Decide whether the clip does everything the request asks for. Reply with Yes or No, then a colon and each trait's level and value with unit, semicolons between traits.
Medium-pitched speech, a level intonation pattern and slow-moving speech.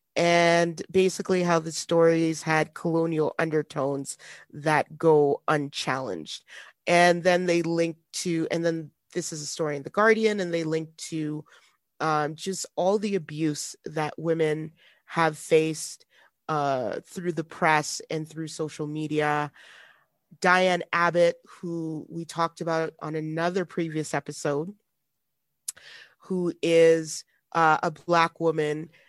Yes: medium, 165 Hz; narrow, 1.9 semitones; slow, 130 wpm